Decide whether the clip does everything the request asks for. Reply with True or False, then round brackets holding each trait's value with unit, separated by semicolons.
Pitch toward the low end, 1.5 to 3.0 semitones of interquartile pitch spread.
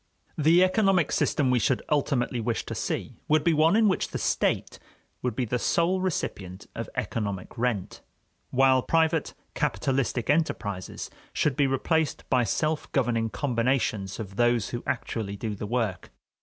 False (125 Hz; 5.4 semitones)